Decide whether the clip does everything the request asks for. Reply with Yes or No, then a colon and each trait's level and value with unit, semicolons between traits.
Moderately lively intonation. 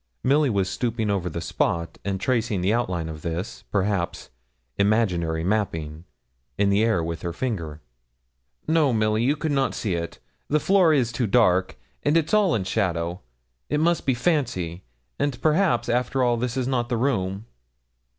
No: wide, 6.4 semitones